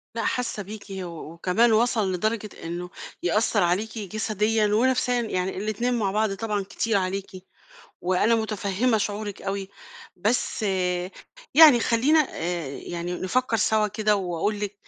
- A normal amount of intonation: Yes, average, 3.1 semitones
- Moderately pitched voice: No, high, 210 Hz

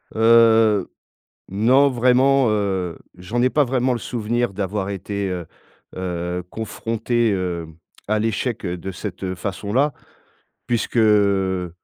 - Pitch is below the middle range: Yes, low, 105 Hz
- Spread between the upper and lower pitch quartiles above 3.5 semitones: Yes, average, 4.1 semitones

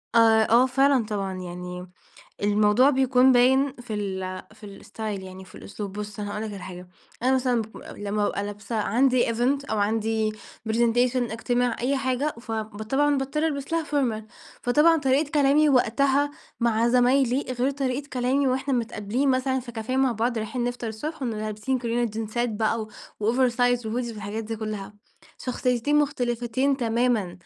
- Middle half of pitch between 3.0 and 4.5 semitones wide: Yes, average, 3.5 semitones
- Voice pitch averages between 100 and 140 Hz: No, high, 240 Hz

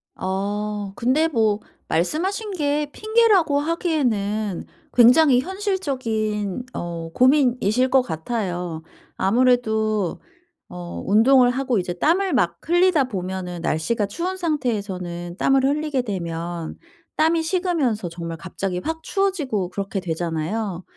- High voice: Yes, high, 230 Hz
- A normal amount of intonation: No, wide, 8.2 semitones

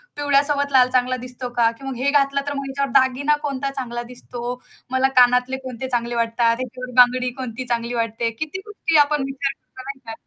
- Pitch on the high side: Yes, very high, 255 Hz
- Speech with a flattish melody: Yes, narrow, 2.2 semitones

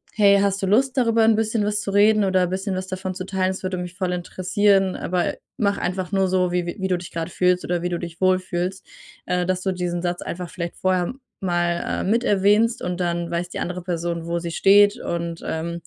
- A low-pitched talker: No, medium, 185 Hz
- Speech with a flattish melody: Yes, narrow, 2.2 semitones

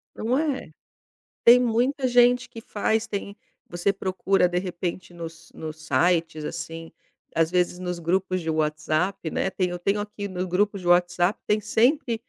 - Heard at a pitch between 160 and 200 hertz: Yes, medium, 185 Hz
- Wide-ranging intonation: No, average, 4.1 semitones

